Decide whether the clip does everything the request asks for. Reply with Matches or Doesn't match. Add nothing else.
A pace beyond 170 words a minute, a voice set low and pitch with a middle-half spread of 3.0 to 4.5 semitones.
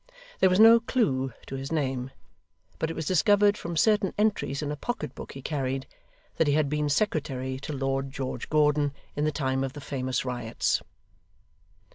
Doesn't match